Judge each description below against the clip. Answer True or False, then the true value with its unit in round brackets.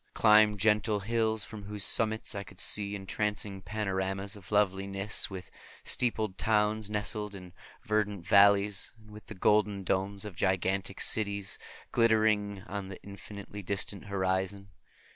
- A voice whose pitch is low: True (100 Hz)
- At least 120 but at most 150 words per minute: True (140 wpm)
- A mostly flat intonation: True (1.5 semitones)